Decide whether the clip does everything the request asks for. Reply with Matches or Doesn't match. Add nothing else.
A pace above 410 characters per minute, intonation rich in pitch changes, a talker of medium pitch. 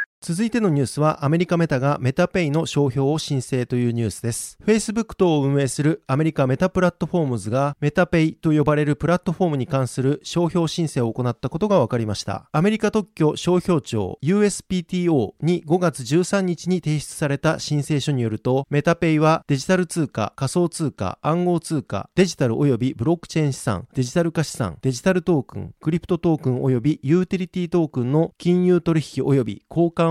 Doesn't match